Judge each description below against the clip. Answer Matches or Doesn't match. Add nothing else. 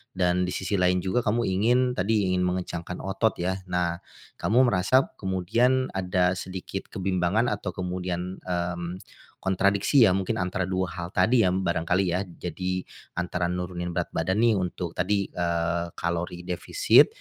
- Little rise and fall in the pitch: Matches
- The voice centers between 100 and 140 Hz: Doesn't match